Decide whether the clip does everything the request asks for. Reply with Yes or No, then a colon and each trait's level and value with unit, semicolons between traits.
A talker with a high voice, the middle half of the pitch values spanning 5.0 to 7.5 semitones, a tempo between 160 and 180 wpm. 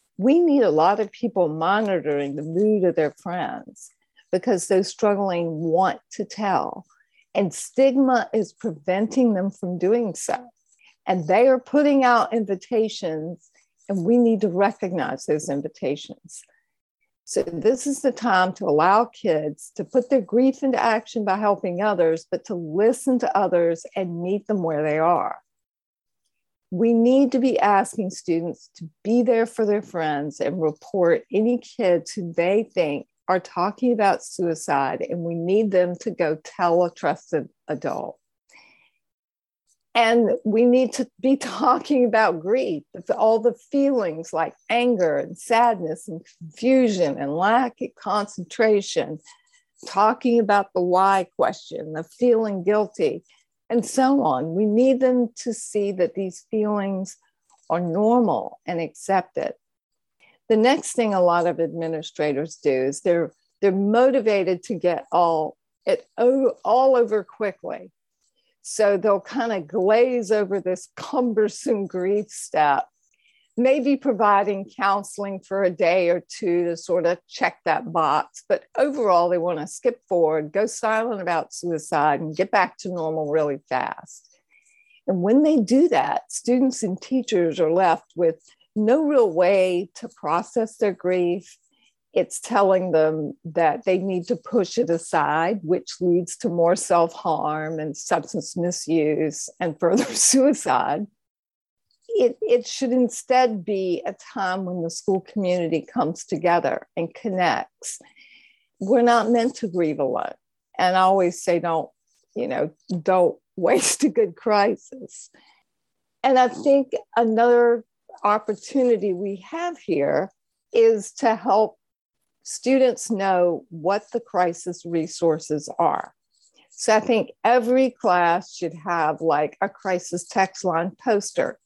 No: high, 200 Hz; wide, 5.5 semitones; average, 140 wpm